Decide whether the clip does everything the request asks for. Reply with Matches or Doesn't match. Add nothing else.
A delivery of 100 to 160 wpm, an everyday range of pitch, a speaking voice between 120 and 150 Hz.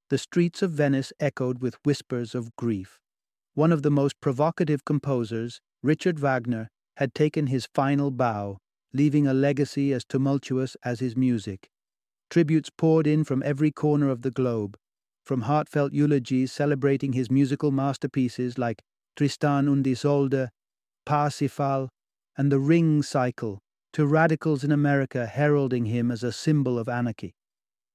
Matches